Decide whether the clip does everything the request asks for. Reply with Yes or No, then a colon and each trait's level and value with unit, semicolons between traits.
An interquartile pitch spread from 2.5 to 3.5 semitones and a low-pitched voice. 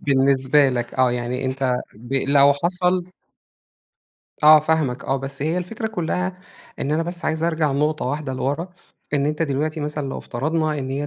No: average, 3.1 semitones; medium, 145 Hz